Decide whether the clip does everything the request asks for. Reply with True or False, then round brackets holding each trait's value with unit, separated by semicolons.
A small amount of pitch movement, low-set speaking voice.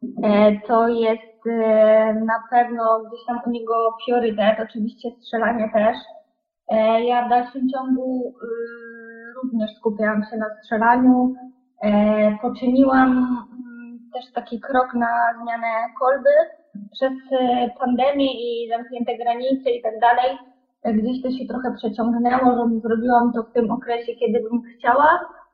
False (1.8 semitones; 235 Hz)